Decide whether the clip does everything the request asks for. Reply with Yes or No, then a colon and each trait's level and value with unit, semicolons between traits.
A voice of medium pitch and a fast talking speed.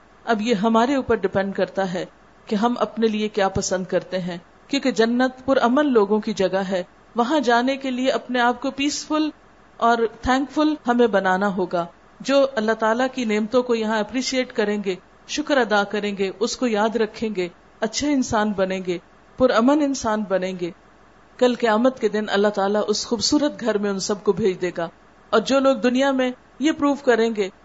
No: high, 225 Hz; fast, 195 wpm